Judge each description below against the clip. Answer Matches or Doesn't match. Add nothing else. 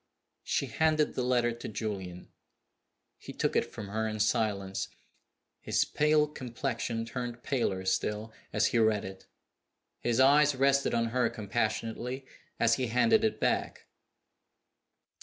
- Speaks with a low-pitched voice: Matches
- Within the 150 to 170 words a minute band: Doesn't match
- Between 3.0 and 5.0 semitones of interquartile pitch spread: Matches